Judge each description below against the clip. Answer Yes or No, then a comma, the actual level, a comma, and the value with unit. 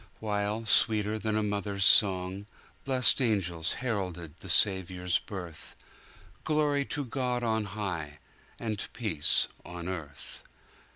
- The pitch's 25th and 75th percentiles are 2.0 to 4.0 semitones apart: Yes, average, 3.6 semitones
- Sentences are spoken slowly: Yes, slow, 105 wpm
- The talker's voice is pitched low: Yes, low, 100 Hz